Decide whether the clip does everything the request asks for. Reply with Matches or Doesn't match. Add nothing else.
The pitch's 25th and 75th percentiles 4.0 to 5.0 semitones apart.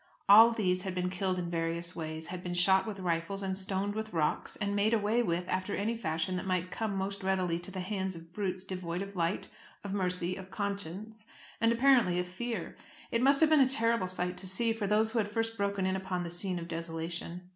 Doesn't match